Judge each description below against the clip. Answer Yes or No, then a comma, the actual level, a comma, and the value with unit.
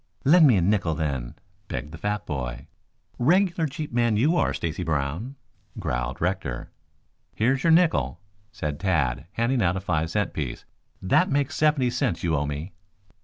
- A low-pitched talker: Yes, very low, 95 Hz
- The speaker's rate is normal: Yes, average, 165 wpm